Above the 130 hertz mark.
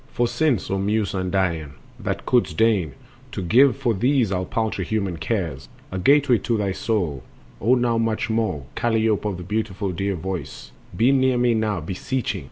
No: low, 105 Hz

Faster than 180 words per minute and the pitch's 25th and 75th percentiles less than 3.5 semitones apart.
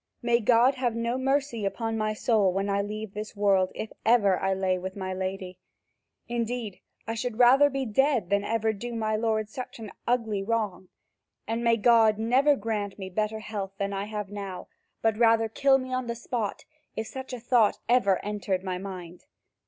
Yes: average, 190 wpm; average, 3.1 semitones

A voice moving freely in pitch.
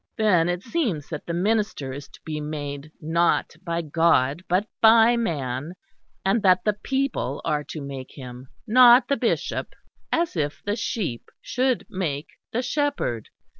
Yes: wide, 7.4 semitones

